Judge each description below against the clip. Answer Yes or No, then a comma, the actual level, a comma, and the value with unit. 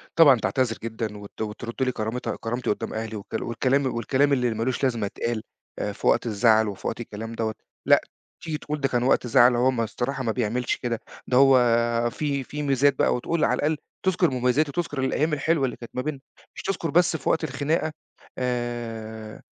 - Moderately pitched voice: No, low, 125 Hz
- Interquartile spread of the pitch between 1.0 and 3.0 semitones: No, average, 3.7 semitones